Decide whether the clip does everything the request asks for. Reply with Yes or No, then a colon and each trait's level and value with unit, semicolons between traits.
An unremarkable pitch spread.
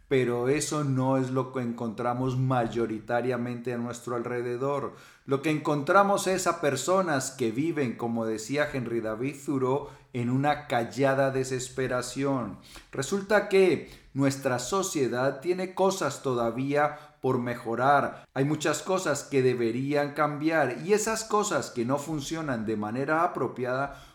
Yes: average, 3.4 semitones